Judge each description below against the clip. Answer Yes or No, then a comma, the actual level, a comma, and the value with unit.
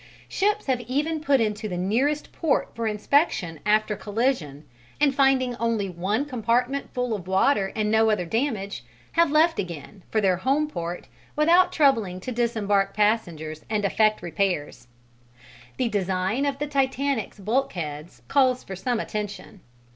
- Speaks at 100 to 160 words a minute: Yes, average, 145 wpm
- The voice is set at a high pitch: Yes, high, 220 Hz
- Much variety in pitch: Yes, wide, 6.0 semitones